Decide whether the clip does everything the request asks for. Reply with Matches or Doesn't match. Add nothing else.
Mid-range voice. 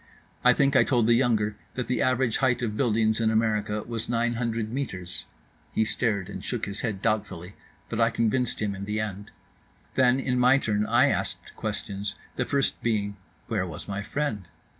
Doesn't match